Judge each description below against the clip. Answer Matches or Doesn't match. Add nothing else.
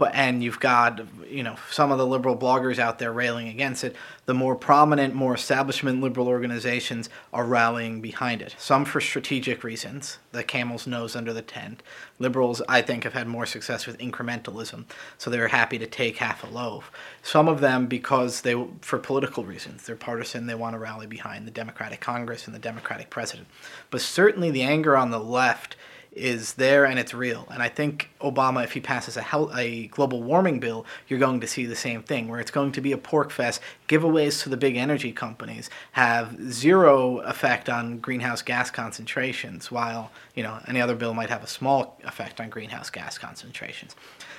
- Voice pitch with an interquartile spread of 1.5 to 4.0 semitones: Matches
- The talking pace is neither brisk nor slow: Matches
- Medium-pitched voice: Doesn't match